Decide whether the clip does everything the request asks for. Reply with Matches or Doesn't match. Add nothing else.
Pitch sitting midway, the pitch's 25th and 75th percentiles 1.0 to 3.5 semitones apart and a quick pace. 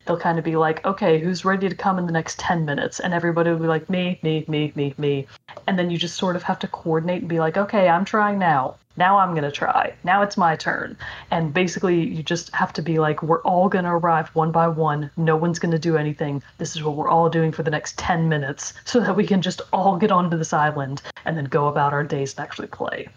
Matches